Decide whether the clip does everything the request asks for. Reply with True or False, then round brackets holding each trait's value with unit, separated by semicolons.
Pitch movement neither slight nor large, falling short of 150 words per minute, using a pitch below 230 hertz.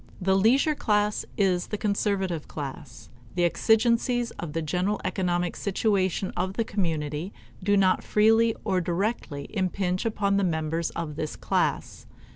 True (3.5 semitones; 140 wpm; 190 Hz)